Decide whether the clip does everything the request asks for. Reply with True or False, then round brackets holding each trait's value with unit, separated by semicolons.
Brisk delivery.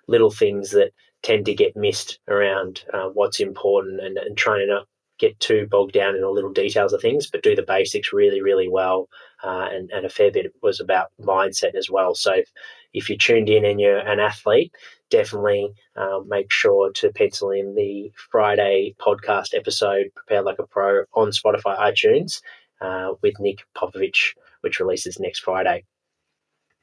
False (180 wpm)